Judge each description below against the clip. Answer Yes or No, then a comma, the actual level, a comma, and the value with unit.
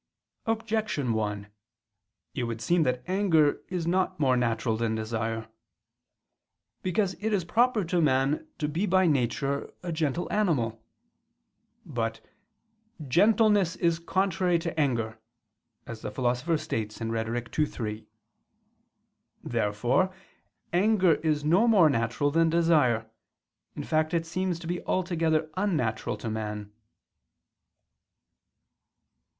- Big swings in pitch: Yes, wide, 7.5 semitones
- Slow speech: Yes, slow, 115 wpm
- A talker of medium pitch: Yes, medium, 155 Hz